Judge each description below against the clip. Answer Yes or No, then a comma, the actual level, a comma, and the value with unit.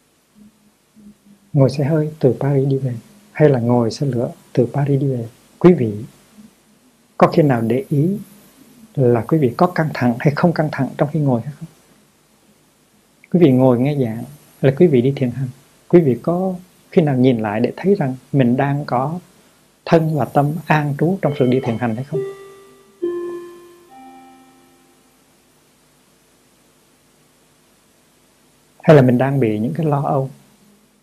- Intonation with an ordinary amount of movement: No, wide, 7.1 semitones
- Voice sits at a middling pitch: Yes, medium, 150 Hz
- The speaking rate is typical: No, slow, 160 wpm